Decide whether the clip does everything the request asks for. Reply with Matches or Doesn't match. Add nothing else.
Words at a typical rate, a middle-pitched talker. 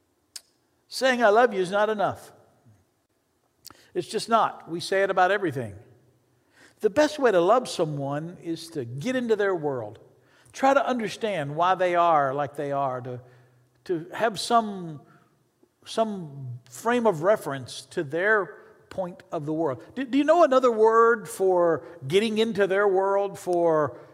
Matches